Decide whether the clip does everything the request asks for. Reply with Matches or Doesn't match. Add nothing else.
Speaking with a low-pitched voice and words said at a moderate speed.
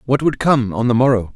Doesn't match